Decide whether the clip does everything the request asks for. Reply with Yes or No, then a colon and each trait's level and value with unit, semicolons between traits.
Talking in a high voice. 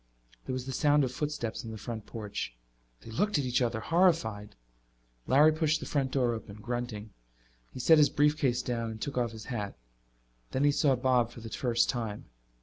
No: low, 125 Hz